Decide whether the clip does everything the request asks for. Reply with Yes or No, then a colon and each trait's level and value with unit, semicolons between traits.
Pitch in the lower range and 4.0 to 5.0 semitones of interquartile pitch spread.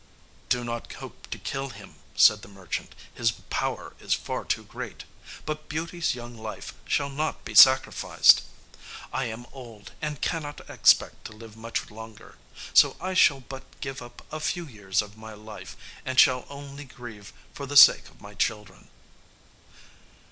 Yes: low, 120 Hz; average, 4.6 semitones